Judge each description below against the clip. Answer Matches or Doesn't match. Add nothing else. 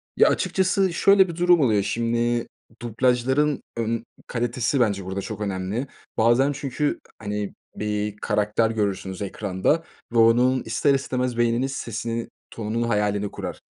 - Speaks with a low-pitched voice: Matches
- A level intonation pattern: Doesn't match